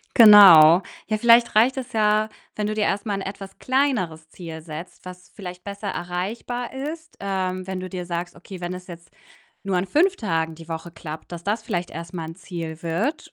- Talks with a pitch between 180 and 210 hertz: Yes, medium, 185 Hz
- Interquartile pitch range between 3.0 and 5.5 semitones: Yes, average, 4.0 semitones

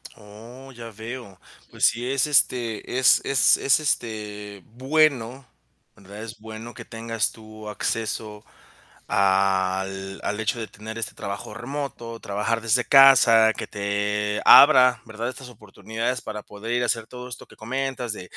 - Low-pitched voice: Yes, low, 115 Hz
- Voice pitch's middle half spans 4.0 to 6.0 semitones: No, average, 3.0 semitones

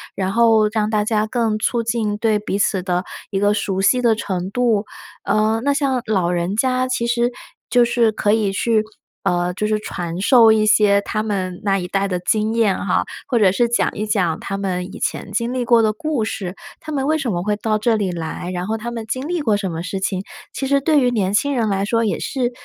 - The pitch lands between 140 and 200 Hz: No, high, 215 Hz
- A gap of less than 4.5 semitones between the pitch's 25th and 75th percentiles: Yes, average, 3.3 semitones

